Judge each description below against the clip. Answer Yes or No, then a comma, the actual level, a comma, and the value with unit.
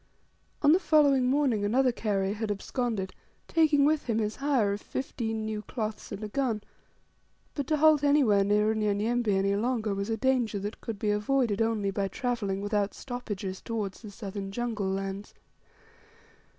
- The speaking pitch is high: Yes, high, 220 Hz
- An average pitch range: Yes, average, 3.9 semitones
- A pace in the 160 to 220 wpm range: Yes, average, 165 wpm